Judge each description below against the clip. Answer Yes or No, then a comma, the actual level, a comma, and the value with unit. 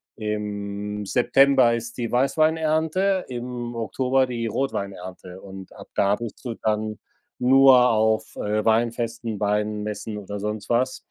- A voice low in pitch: Yes, low, 115 Hz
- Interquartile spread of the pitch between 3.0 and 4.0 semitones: Yes, average, 3.3 semitones